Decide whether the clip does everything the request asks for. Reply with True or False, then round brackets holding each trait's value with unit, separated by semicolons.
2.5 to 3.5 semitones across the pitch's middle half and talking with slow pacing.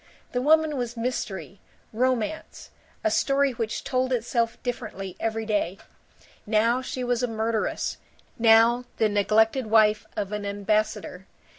True (2.8 semitones; 130 wpm)